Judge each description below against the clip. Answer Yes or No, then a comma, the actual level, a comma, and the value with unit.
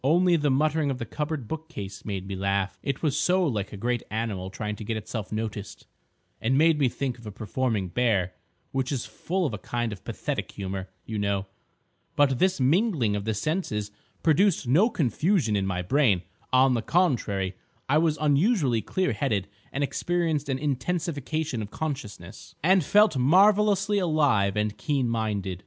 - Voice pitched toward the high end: No, low, 130 Hz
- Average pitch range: No, wide, 7.1 semitones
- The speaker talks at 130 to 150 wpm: No, average, 170 wpm